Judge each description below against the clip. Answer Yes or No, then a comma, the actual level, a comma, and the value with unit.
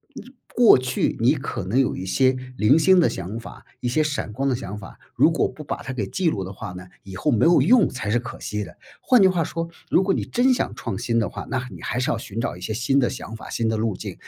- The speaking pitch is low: Yes, low, 125 Hz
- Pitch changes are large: Yes, wide, 6.6 semitones